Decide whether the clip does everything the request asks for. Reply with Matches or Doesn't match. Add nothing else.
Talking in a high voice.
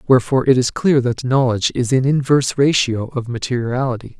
Doesn't match